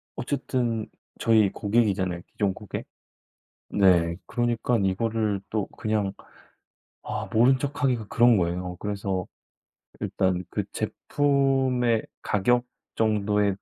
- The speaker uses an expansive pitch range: No, average, 3.7 semitones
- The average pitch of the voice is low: Yes, low, 110 Hz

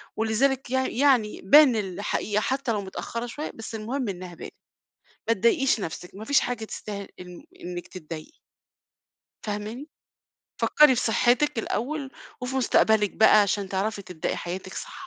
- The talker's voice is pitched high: Yes, high, 220 Hz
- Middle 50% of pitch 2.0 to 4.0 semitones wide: No, average, 4.7 semitones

